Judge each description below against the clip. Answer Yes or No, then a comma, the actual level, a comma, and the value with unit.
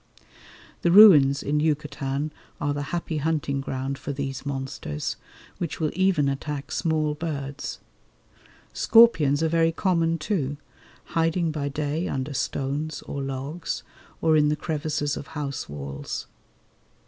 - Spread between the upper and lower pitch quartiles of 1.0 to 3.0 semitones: Yes, average, 2.7 semitones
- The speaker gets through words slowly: Yes, slow, 130 wpm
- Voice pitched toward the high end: No, medium, 150 Hz